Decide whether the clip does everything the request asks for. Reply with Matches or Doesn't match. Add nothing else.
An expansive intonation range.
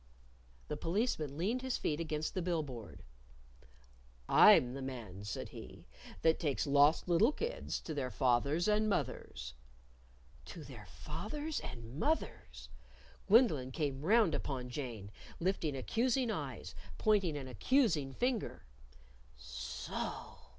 Matches